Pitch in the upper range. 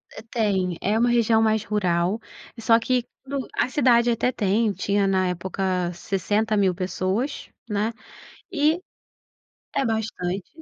Yes: high, 215 Hz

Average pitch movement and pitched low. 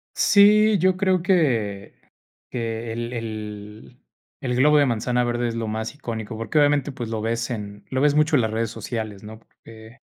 Yes: average, 4.6 semitones; low, 115 Hz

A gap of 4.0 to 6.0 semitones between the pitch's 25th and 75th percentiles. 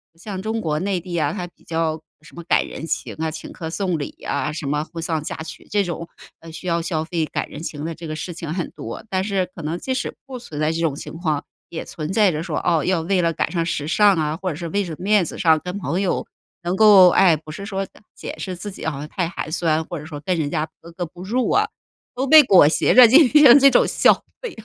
No: average, 3.5 semitones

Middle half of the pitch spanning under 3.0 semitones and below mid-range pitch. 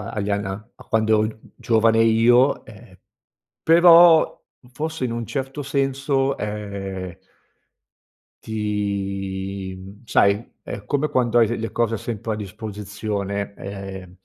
No: average, 3.6 semitones; low, 110 Hz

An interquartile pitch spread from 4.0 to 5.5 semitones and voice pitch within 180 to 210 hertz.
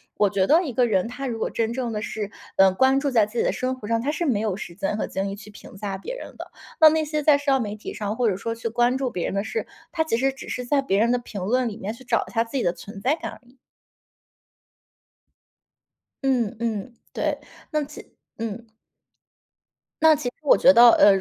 No: average, 4.3 semitones; high, 235 Hz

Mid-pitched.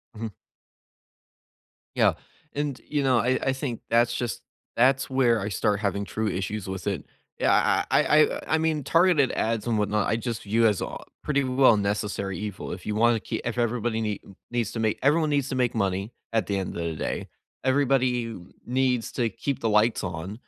No: low, 115 Hz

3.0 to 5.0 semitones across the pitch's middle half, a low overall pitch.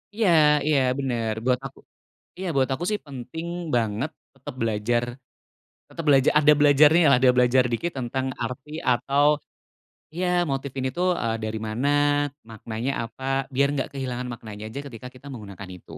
Yes: average, 3.5 semitones; low, 130 Hz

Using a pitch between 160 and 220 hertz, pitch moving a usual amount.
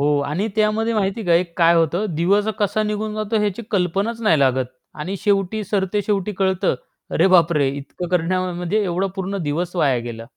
Yes: medium, 185 Hz; average, 3.8 semitones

